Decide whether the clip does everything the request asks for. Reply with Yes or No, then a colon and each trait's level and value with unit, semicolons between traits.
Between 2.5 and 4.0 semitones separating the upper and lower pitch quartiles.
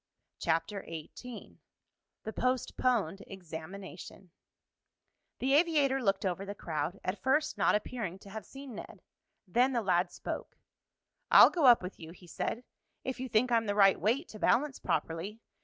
No: wide, 5.6 semitones